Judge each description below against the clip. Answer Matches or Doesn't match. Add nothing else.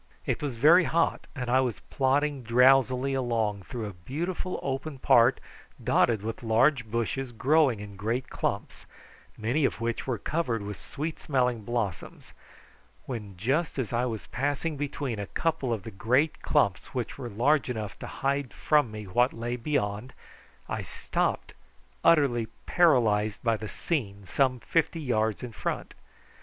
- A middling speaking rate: Matches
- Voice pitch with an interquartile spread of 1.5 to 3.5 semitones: Doesn't match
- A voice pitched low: Matches